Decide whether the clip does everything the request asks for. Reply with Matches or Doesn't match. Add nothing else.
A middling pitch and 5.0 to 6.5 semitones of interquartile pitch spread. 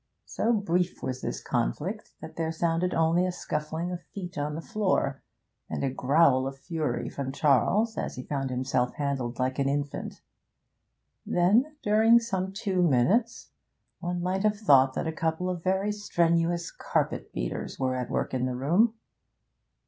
Matches